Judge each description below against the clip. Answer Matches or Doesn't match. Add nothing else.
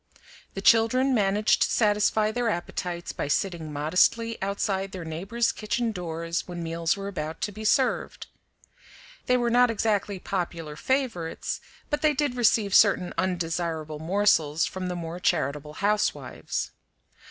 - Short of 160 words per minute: Matches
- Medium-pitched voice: Doesn't match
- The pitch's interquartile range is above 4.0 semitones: Matches